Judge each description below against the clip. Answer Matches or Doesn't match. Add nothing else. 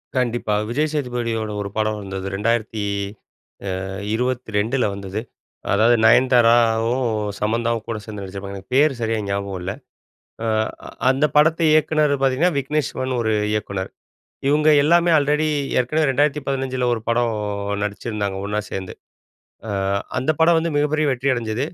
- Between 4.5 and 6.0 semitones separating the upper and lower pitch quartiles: Matches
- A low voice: Matches